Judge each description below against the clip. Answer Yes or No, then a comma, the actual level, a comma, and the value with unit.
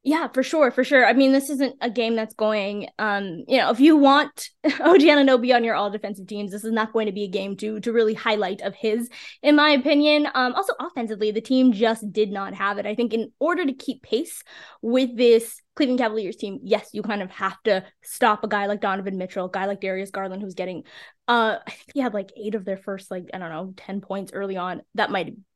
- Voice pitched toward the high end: Yes, high, 220 Hz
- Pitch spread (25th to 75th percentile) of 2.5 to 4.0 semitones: No, average, 4.6 semitones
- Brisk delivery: Yes, fast, 245 wpm